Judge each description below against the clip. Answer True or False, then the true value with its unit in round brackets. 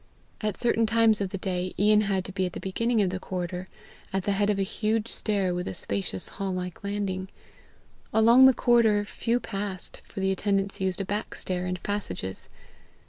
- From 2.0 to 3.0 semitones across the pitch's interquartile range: True (2.4 semitones)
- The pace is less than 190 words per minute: False (195 wpm)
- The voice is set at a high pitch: True (195 Hz)